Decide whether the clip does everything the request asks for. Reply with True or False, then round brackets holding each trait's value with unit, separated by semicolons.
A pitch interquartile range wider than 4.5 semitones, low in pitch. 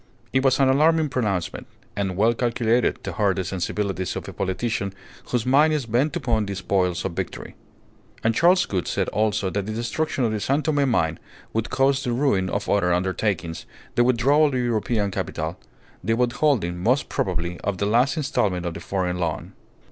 True (5.6 semitones; 110 Hz)